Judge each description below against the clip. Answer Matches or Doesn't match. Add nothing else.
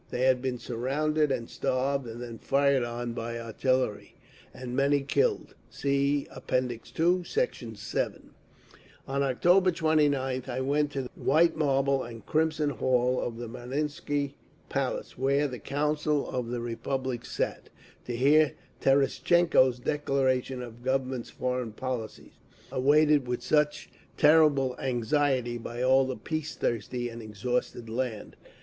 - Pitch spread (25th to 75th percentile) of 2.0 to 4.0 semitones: Matches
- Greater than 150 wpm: Doesn't match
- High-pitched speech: Doesn't match